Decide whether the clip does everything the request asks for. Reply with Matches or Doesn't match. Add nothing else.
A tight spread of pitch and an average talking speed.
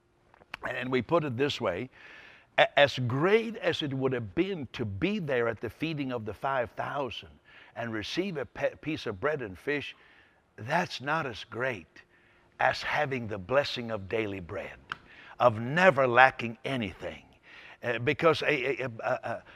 Doesn't match